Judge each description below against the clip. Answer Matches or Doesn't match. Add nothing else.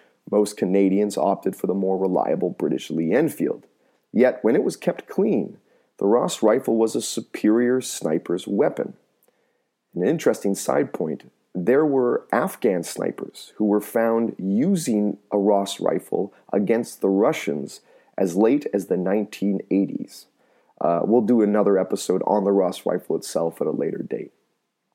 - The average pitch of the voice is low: Matches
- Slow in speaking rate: Doesn't match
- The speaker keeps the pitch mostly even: Matches